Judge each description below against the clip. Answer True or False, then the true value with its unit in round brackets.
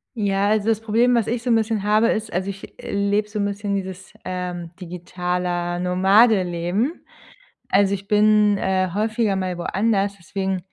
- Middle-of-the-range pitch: False (200 Hz)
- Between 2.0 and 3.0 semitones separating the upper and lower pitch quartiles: True (2.7 semitones)